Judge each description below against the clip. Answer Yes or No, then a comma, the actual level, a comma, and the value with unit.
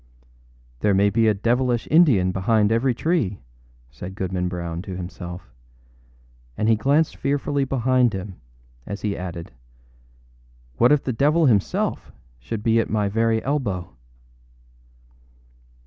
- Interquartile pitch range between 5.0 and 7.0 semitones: Yes, wide, 5.4 semitones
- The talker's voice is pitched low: Yes, low, 110 Hz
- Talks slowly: Yes, slow, 130 wpm